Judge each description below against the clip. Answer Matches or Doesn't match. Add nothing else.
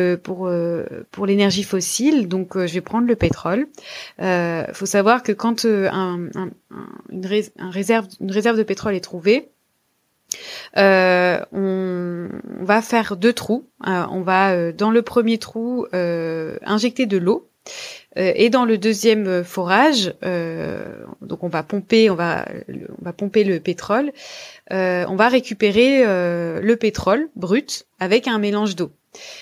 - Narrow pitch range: Doesn't match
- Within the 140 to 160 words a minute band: Matches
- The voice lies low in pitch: Doesn't match